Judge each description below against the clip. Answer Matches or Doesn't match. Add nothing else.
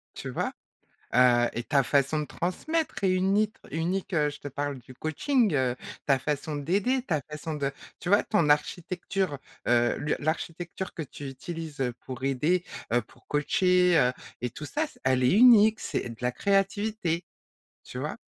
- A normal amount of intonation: Doesn't match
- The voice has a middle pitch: Matches